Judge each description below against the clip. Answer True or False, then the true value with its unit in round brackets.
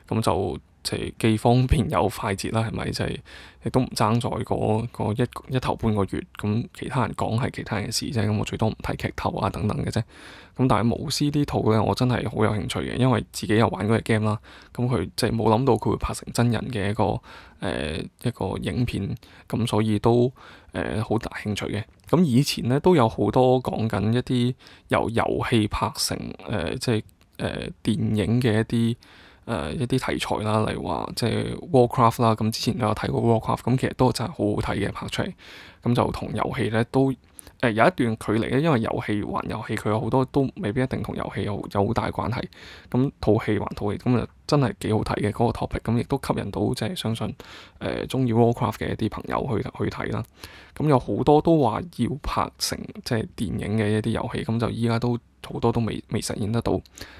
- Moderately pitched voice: False (110 Hz)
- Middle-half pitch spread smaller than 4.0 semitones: True (2.8 semitones)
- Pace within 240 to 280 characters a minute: False (340 characters per minute)